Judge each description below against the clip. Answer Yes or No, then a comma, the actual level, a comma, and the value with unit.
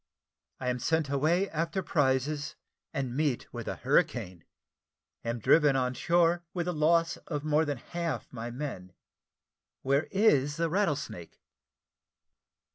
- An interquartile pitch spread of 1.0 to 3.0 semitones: No, average, 4.3 semitones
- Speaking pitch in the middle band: Yes, medium, 150 Hz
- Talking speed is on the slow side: Yes, slow, 130 wpm